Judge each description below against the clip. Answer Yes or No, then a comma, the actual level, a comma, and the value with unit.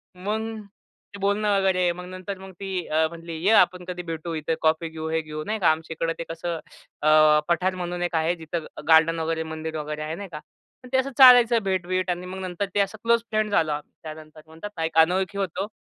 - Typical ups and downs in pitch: Yes, average, 3.2 semitones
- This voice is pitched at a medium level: Yes, medium, 175 Hz